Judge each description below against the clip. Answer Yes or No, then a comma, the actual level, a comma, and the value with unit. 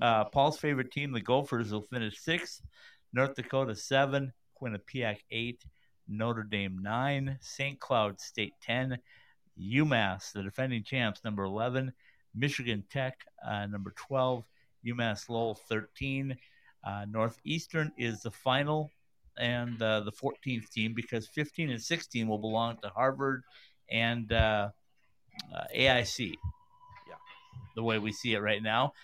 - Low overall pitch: Yes, low, 120 Hz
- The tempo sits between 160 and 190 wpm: No, slow, 135 wpm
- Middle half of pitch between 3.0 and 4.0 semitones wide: Yes, average, 3.7 semitones